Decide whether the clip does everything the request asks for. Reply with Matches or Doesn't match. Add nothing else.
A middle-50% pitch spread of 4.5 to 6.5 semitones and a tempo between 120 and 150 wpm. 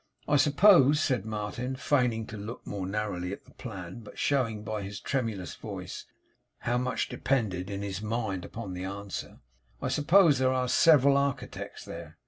Doesn't match